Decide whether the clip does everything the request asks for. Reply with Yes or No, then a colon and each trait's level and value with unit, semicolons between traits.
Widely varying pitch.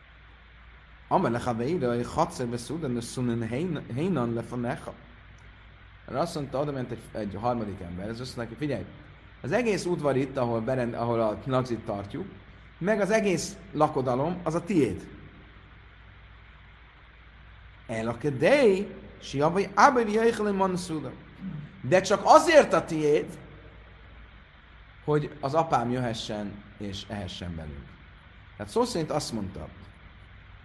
Yes: wide, 7.4 semitones